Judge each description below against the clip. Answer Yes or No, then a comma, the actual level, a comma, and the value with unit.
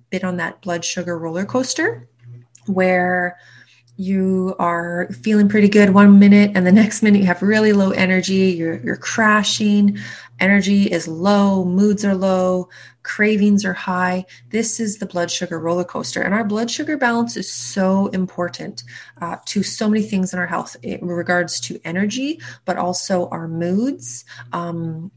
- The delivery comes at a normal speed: Yes, average, 160 wpm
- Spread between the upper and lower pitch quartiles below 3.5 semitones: Yes, average, 2.8 semitones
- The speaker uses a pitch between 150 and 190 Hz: Yes, medium, 185 Hz